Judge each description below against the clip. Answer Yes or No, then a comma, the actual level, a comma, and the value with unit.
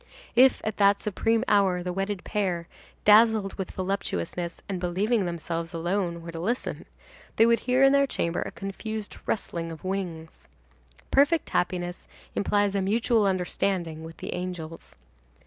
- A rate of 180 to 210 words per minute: No, average, 145 wpm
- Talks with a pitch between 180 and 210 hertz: Yes, high, 190 Hz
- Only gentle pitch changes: No, average, 3.6 semitones